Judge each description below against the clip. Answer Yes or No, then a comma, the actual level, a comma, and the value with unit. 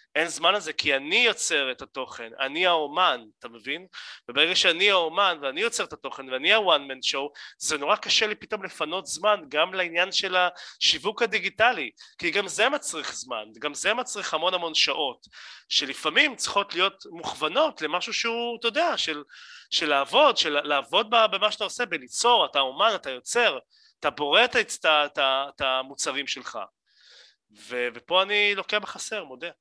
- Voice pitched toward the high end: No, medium, 180 Hz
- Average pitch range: No, wide, 6.9 semitones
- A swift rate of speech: Yes, fast, 160 wpm